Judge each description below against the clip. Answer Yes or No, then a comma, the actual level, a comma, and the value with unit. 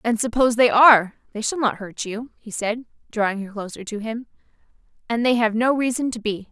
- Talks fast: Yes, fast, 210 wpm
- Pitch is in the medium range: No, high, 225 Hz